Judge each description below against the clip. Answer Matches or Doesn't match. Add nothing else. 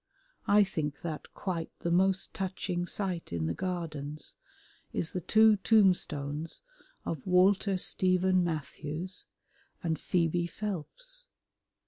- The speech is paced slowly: Matches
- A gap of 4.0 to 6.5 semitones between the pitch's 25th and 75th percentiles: Doesn't match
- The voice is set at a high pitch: Doesn't match